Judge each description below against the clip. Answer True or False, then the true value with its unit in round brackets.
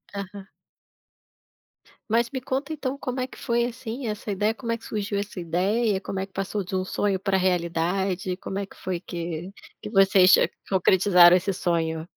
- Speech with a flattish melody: False (3.4 semitones)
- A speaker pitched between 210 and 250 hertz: False (195 Hz)